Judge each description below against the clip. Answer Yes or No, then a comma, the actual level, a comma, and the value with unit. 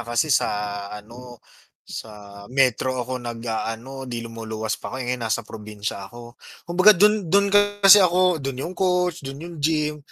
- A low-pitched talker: Yes, low, 130 Hz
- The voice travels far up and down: Yes, wide, 7.3 semitones